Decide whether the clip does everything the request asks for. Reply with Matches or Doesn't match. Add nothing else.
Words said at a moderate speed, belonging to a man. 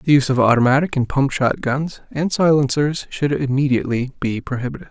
Matches